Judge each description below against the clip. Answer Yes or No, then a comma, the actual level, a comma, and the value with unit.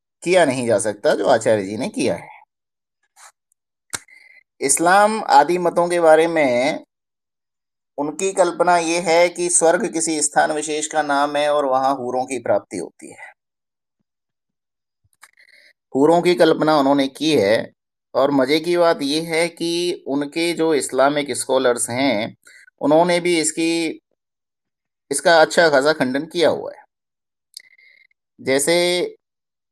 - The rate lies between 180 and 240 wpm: No, average, 125 wpm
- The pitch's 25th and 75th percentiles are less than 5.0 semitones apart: No, wide, 5.5 semitones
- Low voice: No, medium, 165 Hz